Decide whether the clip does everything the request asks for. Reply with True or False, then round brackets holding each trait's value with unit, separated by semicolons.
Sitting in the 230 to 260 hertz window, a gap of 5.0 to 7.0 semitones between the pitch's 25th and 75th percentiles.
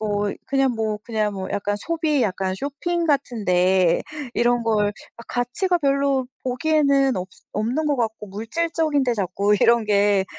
True (235 Hz; 5.3 semitones)